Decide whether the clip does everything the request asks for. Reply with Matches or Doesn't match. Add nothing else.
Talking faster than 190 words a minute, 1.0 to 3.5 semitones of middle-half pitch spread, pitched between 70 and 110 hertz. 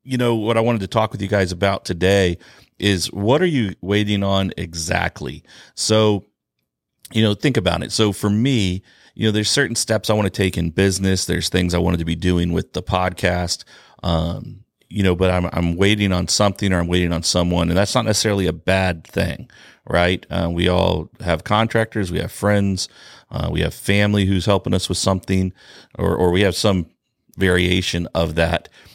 Matches